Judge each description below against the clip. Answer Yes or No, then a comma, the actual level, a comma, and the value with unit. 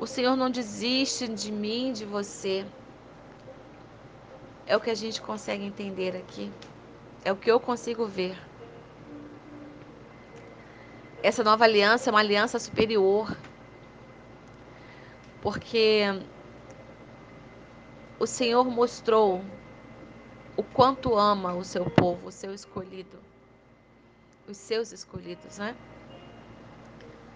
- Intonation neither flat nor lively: Yes, average, 3.6 semitones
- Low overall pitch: No, high, 205 Hz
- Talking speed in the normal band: No, slow, 100 wpm